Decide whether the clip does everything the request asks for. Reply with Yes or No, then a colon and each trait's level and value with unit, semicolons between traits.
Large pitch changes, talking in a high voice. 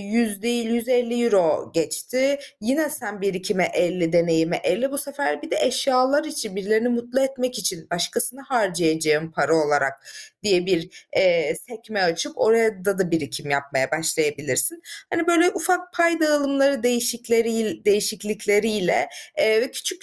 Yes: wide, 7.1 semitones; high, 220 Hz